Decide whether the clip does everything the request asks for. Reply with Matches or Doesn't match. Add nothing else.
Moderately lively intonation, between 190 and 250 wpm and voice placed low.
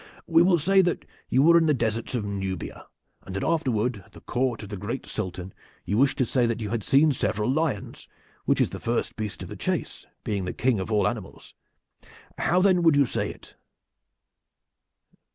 Doesn't match